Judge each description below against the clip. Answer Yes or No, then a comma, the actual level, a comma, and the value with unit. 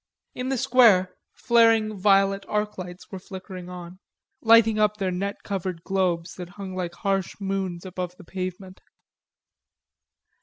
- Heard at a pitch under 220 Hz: Yes, high, 190 Hz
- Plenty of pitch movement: No, narrow, 2.4 semitones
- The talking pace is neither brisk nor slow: No, slow, 130 wpm